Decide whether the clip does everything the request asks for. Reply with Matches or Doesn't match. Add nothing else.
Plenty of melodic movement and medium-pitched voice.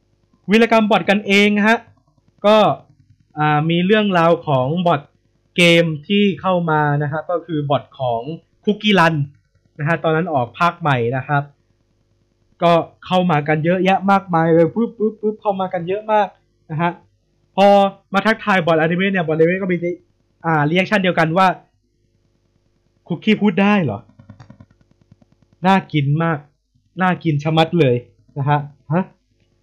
Matches